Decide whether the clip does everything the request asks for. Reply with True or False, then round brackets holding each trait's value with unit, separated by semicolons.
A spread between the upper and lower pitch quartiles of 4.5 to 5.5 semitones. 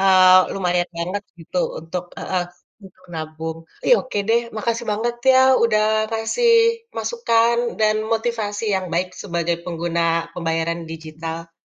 True (5.0 semitones)